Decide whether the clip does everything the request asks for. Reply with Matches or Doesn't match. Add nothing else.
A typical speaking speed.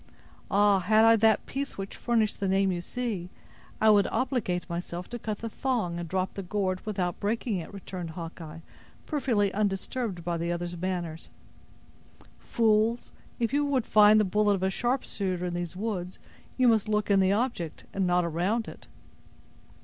Matches